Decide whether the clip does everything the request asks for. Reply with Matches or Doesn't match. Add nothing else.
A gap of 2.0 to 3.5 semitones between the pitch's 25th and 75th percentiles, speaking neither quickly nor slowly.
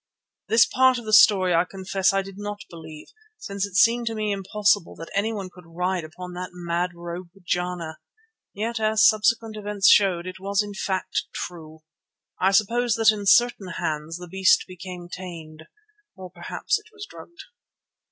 Matches